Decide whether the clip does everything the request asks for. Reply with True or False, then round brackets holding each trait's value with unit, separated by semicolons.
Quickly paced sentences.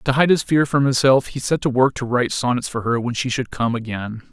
True (280 wpm)